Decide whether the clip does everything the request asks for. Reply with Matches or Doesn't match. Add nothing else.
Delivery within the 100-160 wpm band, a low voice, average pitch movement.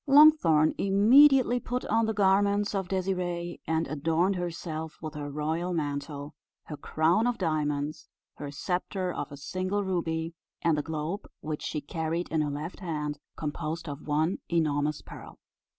Doesn't match